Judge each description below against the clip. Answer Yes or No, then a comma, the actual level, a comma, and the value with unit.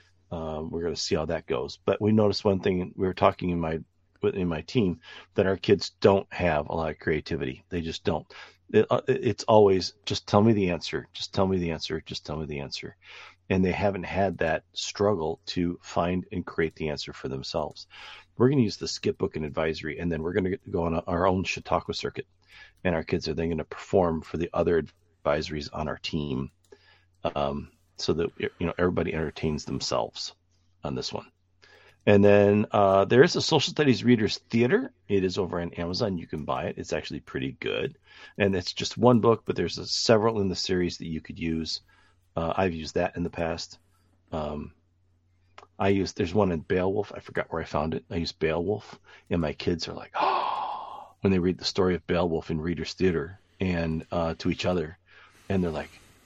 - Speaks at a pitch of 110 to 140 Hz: No, very low, 90 Hz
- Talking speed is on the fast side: Yes, fast, 210 wpm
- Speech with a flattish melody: No, average, 3.0 semitones